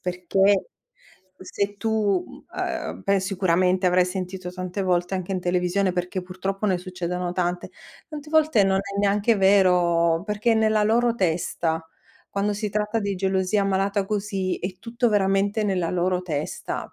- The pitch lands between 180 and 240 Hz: Yes, high, 190 Hz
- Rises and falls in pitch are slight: Yes, narrow, 2.2 semitones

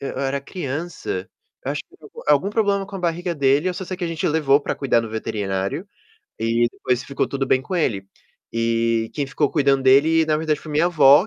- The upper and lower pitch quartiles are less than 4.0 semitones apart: No, average, 4.8 semitones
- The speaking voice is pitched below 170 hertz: Yes, medium, 140 Hz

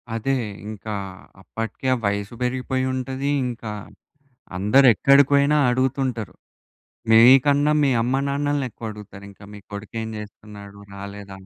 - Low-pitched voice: Yes, low, 120 Hz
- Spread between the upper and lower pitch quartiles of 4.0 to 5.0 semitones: Yes, average, 4.6 semitones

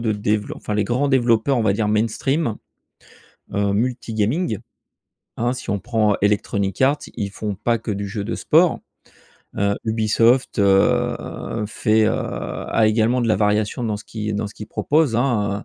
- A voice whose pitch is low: Yes, low, 110 Hz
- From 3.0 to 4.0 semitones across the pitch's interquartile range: No, narrow, 2.5 semitones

